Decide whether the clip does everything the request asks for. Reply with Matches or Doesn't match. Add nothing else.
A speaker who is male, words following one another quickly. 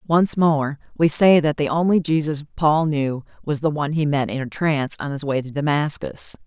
Doesn't match